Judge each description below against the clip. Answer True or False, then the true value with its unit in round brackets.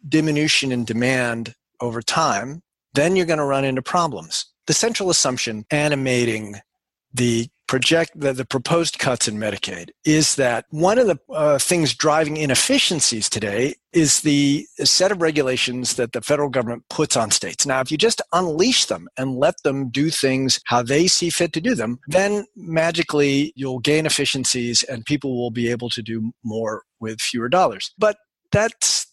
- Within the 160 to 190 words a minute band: True (170 wpm)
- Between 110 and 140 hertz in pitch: True (135 Hz)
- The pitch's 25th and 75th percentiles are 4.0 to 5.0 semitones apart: True (4.6 semitones)